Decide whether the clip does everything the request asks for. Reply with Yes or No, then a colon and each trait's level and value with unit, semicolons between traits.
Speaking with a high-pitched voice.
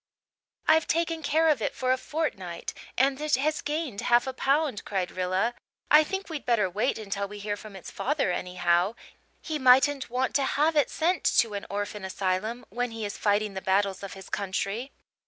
Yes: high, 235 Hz